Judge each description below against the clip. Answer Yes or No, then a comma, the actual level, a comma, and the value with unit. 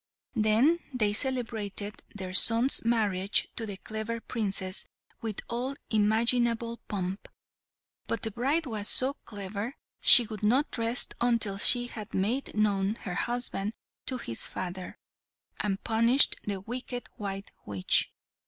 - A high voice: Yes, high, 220 Hz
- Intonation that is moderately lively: Yes, average, 3.1 semitones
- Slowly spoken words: Yes, slow, 130 wpm